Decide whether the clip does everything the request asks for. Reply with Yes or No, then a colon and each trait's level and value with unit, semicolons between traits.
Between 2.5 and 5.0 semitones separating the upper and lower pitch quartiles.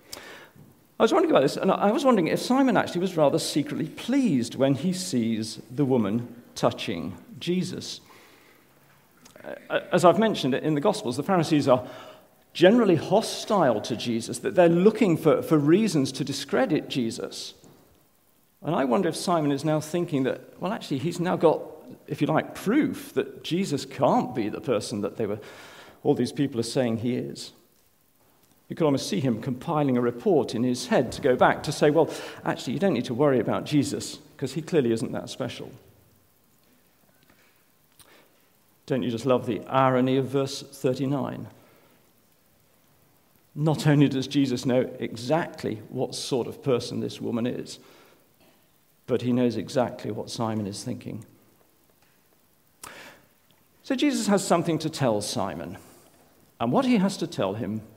No: wide, 5.5 semitones